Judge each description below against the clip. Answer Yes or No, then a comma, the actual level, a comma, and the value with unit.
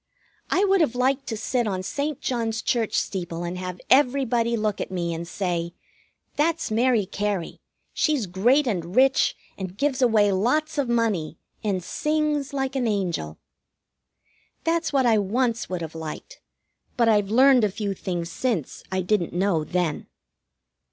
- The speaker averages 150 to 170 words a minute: Yes, average, 160 wpm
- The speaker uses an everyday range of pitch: No, wide, 6.2 semitones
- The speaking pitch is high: Yes, high, 220 Hz